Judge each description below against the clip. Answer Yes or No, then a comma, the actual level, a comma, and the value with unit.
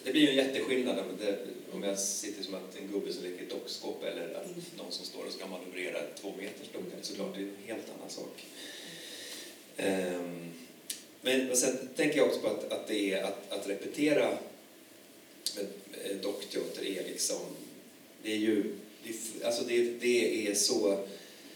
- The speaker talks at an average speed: Yes, average, 160 wpm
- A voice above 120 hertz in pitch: No, low, 115 Hz